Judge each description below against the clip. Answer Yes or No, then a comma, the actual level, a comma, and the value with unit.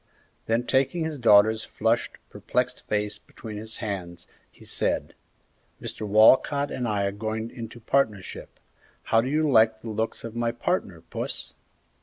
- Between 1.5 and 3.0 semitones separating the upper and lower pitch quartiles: Yes, average, 2.7 semitones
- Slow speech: No, average, 150 wpm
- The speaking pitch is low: Yes, low, 110 Hz